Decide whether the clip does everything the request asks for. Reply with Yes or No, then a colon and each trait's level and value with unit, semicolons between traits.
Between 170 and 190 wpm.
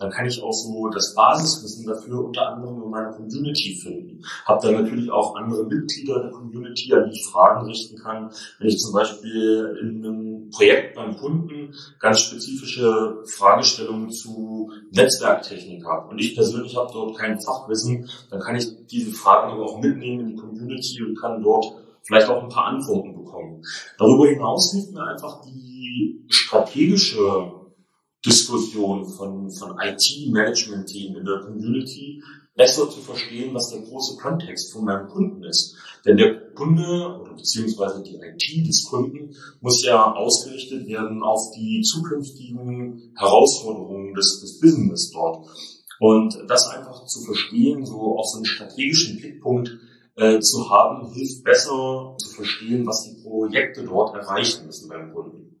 No: average, 155 wpm